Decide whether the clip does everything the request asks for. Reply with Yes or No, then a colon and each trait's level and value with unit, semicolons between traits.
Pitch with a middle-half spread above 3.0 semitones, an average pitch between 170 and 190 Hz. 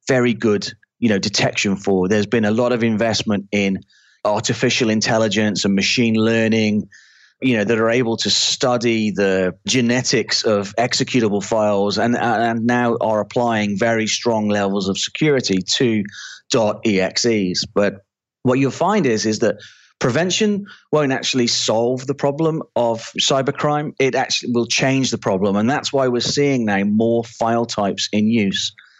No: average, 3.4 semitones; low, 115 Hz